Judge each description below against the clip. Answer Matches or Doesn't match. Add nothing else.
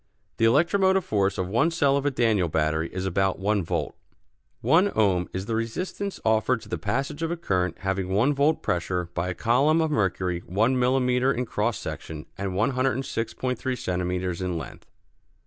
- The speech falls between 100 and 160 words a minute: Doesn't match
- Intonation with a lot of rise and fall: Matches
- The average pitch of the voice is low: Matches